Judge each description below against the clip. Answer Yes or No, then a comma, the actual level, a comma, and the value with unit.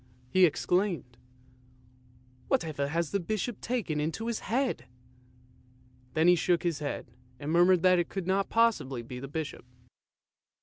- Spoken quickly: No, average, 160 wpm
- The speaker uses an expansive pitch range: Yes, wide, 6.8 semitones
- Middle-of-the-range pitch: Yes, medium, 165 Hz